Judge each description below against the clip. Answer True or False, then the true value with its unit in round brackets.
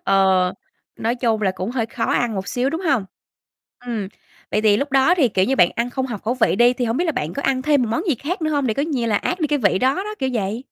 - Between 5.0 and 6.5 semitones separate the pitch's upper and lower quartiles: False (4.6 semitones)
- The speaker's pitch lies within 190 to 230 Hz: False (245 Hz)